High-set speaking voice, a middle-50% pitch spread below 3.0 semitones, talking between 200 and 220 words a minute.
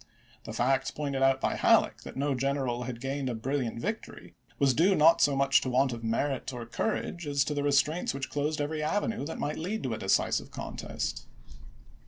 No: medium, 140 Hz; narrow, 2.5 semitones; fast, 205 wpm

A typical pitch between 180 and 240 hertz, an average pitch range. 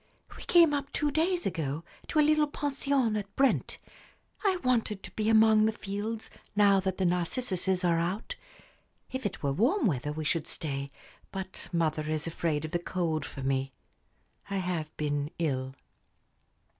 No: high, 190 Hz; wide, 7.2 semitones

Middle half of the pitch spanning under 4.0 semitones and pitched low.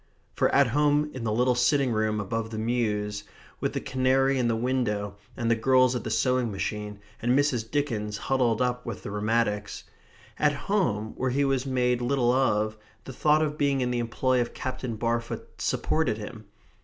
Yes: average, 3.3 semitones; low, 120 Hz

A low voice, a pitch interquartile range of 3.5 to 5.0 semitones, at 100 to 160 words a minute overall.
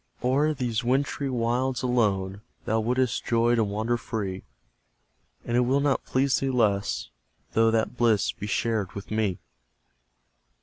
No: low, 115 Hz; average, 2.9 semitones; average, 140 wpm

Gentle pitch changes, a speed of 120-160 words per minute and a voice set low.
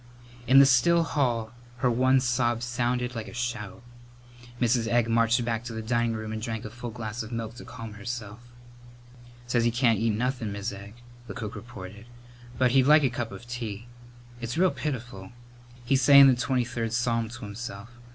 No: narrow, 1.9 semitones; average, 190 wpm; low, 120 Hz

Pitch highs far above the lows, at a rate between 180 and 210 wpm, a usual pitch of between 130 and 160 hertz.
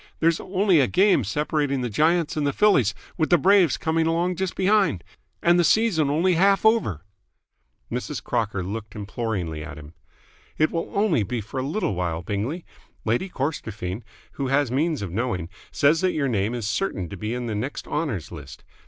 Yes: wide, 8.5 semitones; average, 185 wpm; medium, 140 Hz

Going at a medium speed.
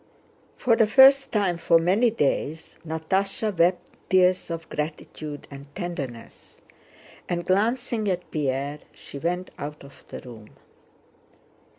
No: slow, 120 wpm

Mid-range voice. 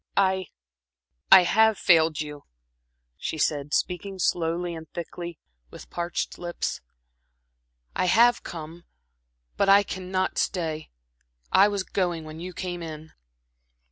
Yes: medium, 175 Hz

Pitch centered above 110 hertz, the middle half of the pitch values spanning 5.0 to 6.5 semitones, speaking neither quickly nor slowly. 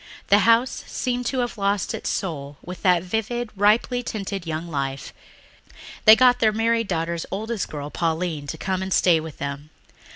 Yes: high, 190 Hz; wide, 5.6 semitones; average, 170 wpm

